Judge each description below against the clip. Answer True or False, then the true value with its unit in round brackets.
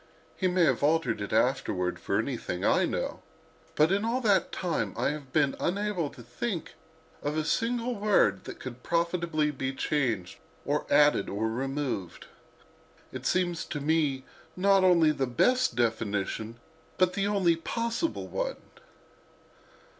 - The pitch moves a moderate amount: False (6.3 semitones)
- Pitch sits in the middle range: True (155 Hz)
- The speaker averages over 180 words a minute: False (145 wpm)